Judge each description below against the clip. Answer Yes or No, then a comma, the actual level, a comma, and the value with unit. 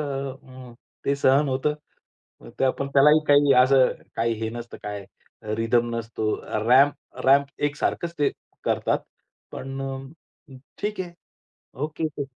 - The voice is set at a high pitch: No, low, 135 Hz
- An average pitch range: Yes, average, 3.2 semitones